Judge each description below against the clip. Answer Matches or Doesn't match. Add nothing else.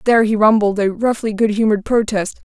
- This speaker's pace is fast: Doesn't match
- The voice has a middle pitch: Doesn't match